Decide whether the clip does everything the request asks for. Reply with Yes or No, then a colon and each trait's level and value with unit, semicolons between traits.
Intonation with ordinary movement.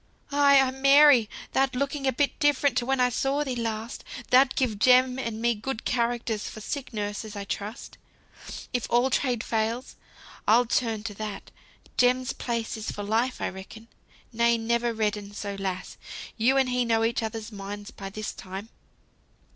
Yes: average, 3.1 semitones